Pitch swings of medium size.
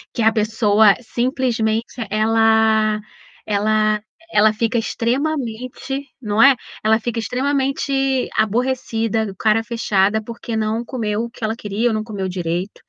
No: narrow, 2.1 semitones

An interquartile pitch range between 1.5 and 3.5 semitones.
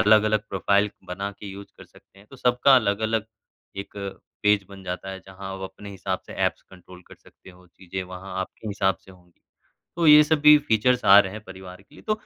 Yes: narrow, 2.4 semitones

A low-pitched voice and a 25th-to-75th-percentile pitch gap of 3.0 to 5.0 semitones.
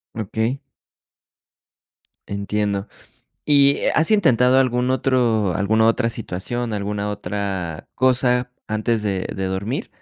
Yes: low, 110 Hz; average, 3.7 semitones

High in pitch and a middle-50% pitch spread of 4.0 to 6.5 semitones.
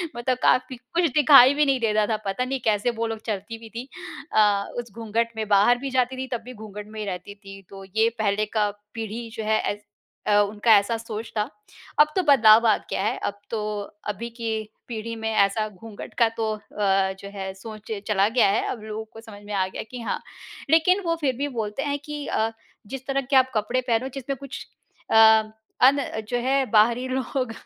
No: high, 225 Hz; average, 3.3 semitones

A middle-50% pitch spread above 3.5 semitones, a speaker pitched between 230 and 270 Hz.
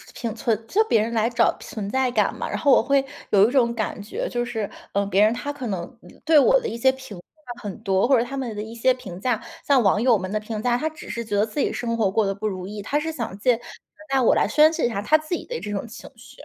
Yes: average, 4.2 semitones; high, 235 Hz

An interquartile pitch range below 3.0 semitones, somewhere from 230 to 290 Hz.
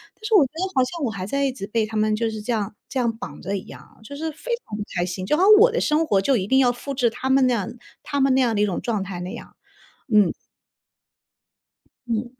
No: average, 4.8 semitones; high, 235 Hz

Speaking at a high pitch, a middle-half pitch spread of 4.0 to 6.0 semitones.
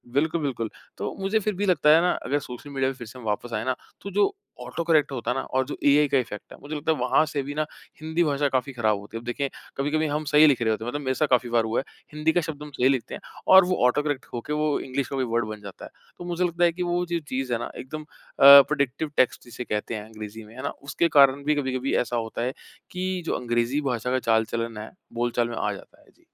No: low, 135 Hz; average, 4.3 semitones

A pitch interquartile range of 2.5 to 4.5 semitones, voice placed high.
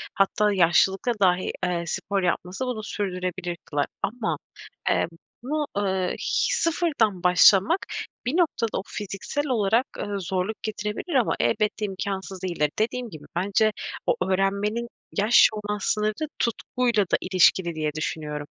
Yes: average, 3.7 semitones; high, 200 Hz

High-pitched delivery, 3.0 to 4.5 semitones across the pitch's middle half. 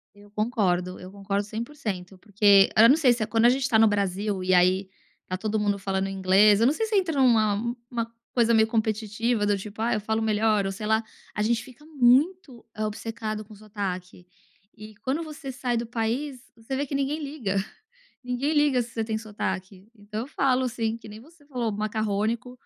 Yes: high, 220 Hz; average, 3.4 semitones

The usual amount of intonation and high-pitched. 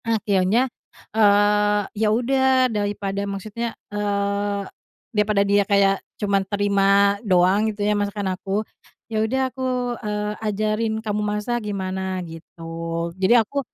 No: narrow, 1.4 semitones; high, 205 Hz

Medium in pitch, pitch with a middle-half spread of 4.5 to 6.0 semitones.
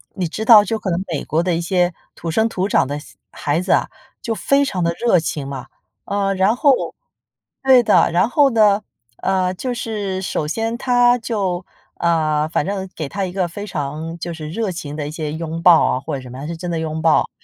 Yes: medium, 180 Hz; average, 4.8 semitones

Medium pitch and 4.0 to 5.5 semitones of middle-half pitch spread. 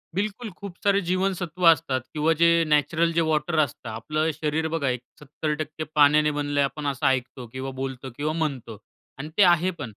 No: medium, 150 Hz; average, 3.4 semitones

